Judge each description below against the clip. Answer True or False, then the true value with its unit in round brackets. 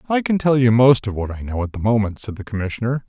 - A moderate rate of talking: False (290 wpm)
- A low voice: True (115 Hz)